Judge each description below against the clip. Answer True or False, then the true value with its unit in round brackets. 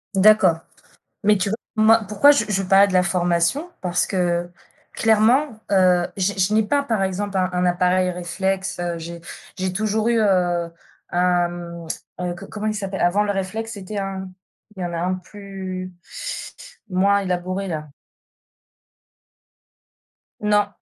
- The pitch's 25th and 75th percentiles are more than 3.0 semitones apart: False (2.7 semitones)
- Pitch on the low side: False (190 Hz)